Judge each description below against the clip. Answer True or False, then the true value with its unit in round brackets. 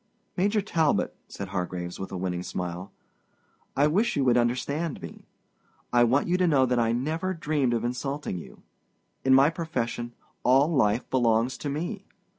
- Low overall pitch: True (130 Hz)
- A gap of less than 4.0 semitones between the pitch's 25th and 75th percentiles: False (5.2 semitones)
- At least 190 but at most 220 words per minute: False (165 wpm)